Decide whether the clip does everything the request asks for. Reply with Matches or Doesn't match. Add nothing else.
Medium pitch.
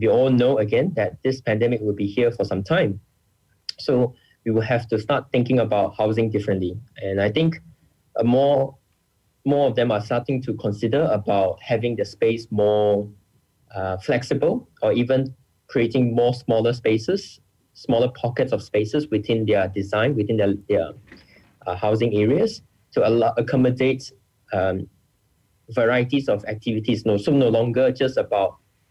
Doesn't match